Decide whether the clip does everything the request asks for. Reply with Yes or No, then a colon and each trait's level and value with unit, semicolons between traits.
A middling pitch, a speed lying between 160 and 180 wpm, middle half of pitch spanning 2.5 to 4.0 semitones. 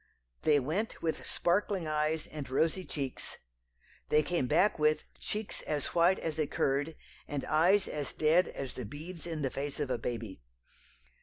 Yes: medium, 155 Hz; average, 165 wpm; average, 3.3 semitones